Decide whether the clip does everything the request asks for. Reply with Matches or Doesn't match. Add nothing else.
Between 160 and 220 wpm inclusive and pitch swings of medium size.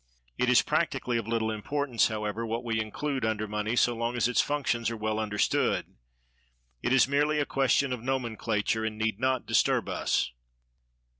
Matches